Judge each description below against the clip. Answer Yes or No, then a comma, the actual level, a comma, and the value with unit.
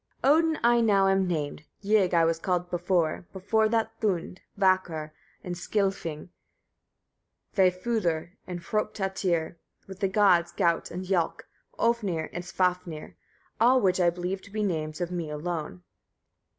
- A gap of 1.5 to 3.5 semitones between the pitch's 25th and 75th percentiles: Yes, average, 2.9 semitones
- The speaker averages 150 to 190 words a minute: No, average, 140 wpm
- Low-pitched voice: No, medium, 180 Hz